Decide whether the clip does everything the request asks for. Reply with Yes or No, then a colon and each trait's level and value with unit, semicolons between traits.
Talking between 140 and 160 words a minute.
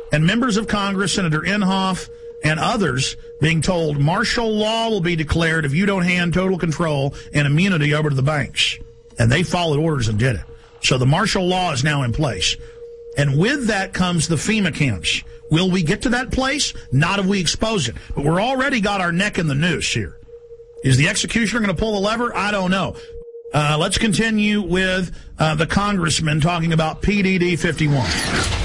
No: average, 195 wpm